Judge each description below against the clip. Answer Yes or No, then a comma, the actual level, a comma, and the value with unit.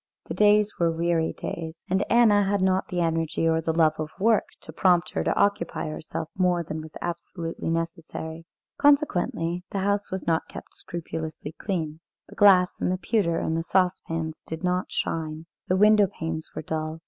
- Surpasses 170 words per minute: Yes, average, 180 wpm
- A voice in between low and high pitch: Yes, medium, 170 Hz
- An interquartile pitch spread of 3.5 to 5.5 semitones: No, average, 2.8 semitones